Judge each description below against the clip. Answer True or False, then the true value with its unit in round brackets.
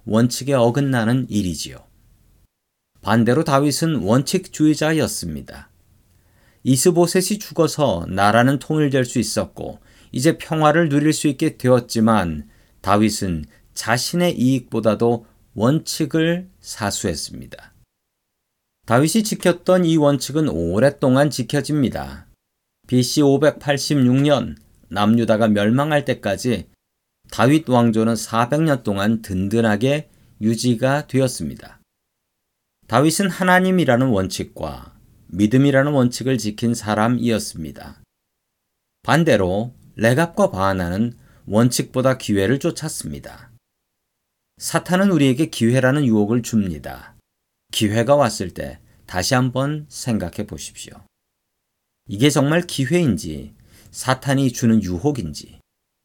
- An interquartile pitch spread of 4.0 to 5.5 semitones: True (5.2 semitones)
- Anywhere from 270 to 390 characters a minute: False (250 characters per minute)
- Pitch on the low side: True (125 Hz)